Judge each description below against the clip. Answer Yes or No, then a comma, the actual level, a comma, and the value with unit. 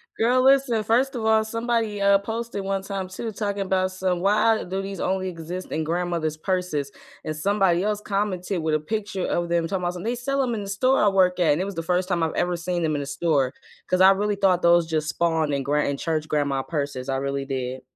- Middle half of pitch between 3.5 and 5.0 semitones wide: Yes, average, 4.3 semitones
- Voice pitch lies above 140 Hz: Yes, medium, 185 Hz